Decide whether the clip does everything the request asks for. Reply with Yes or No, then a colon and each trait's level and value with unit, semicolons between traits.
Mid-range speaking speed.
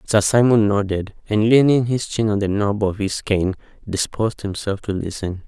Yes: average, 185 wpm